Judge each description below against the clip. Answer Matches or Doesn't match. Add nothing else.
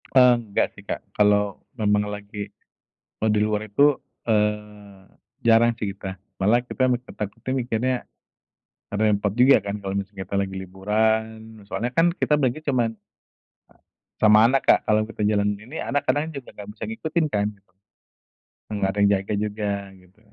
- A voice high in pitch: Doesn't match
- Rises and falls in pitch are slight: Doesn't match